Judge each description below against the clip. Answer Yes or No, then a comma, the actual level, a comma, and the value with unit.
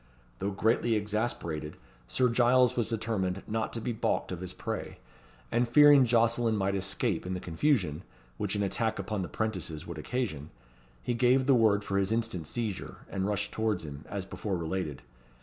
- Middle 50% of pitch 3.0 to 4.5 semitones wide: Yes, average, 4.1 semitones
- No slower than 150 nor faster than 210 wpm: Yes, average, 175 wpm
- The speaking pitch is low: Yes, low, 105 Hz